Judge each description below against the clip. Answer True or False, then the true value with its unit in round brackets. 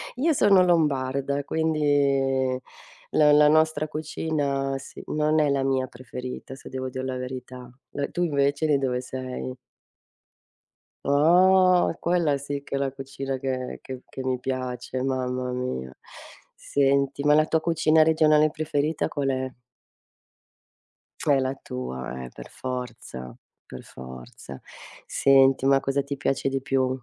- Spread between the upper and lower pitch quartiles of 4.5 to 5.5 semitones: False (2.6 semitones)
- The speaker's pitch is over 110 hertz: True (135 Hz)